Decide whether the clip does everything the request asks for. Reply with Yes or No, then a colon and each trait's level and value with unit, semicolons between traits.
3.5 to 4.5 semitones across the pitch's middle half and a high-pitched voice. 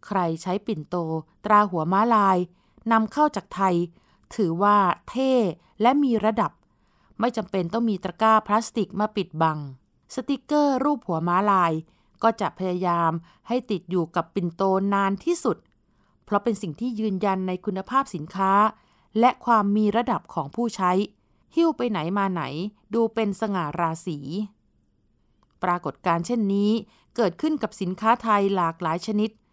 Yes: average, 4.1 semitones; high, 200 Hz